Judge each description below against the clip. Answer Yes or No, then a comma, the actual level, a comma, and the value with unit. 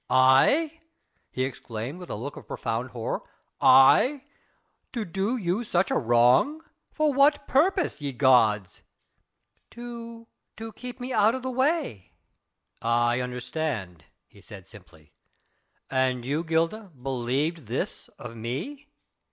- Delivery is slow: Yes, slow, 125 wpm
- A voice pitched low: No, medium, 145 Hz